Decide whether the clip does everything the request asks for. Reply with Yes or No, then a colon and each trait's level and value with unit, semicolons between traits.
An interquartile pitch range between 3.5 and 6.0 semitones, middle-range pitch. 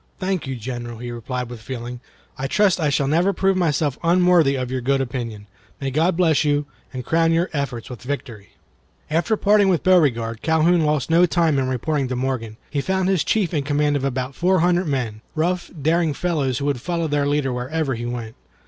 Yes: average, 5.0 semitones; medium, 145 Hz